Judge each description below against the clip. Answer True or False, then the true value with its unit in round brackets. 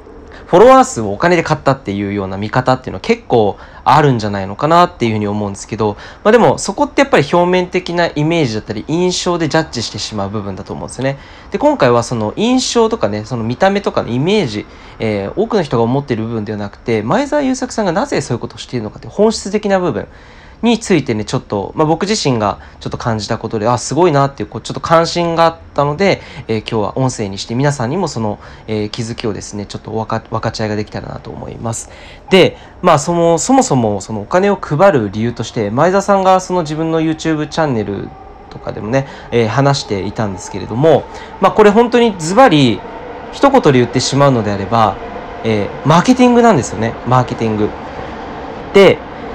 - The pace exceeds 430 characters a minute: True (460 characters per minute)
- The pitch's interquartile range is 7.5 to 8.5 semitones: True (8.2 semitones)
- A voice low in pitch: True (130 Hz)